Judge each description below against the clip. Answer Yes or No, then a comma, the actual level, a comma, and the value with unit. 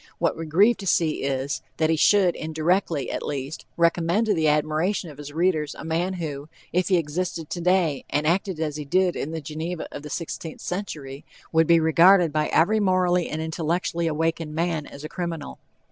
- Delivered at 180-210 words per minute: Yes, average, 190 wpm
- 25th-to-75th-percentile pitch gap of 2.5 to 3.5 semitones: Yes, average, 2.8 semitones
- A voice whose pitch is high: No, medium, 165 Hz